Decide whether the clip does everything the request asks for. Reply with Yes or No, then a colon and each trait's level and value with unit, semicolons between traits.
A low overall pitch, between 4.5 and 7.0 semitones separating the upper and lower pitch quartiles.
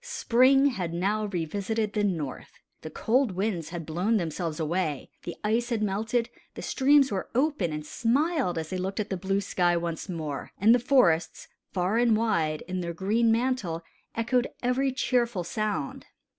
No: high, 200 Hz; wide, 5.6 semitones